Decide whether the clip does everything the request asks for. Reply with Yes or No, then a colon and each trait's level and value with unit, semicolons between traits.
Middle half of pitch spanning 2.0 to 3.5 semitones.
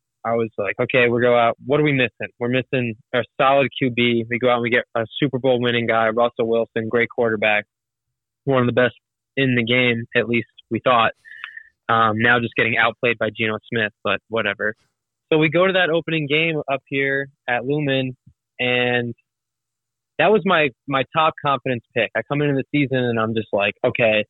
Yes: average, 3.0 semitones